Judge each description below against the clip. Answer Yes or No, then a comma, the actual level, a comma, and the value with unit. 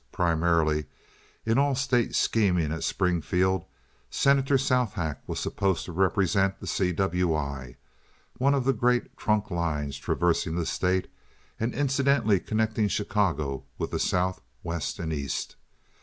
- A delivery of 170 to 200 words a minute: No, slow, 135 wpm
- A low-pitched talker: Yes, very low, 95 Hz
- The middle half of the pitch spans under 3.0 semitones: No, wide, 5.4 semitones